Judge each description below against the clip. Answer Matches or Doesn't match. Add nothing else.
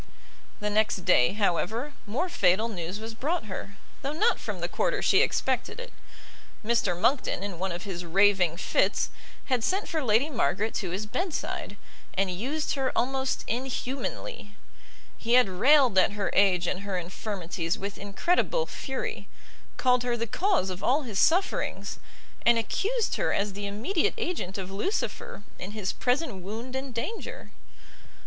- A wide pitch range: Matches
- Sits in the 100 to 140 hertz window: Doesn't match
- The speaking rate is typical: Matches